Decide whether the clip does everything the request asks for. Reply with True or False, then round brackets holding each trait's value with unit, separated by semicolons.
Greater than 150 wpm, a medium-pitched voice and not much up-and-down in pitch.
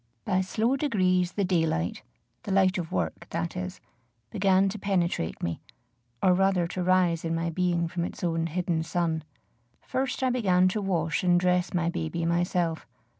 True (170 wpm; 180 Hz; 2.1 semitones)